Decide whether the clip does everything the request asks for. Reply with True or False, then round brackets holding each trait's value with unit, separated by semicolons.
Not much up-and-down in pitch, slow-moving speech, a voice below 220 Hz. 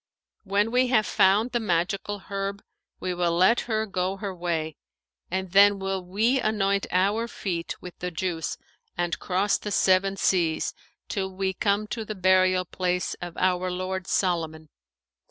False (2.1 semitones; 155 wpm; 190 Hz)